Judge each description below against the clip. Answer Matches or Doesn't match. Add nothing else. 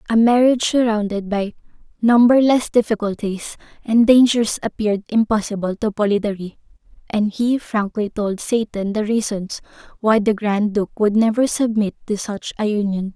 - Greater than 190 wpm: Doesn't match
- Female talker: Matches